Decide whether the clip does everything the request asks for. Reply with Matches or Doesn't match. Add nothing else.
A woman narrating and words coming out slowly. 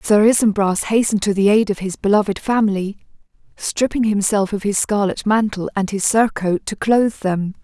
Doesn't match